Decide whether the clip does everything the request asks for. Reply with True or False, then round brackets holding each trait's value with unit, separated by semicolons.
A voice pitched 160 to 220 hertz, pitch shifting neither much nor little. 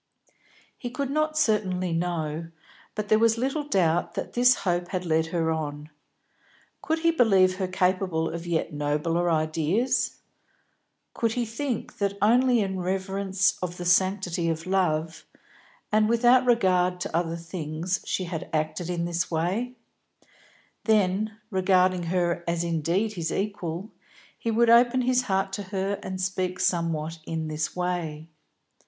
True (185 Hz; 4.3 semitones)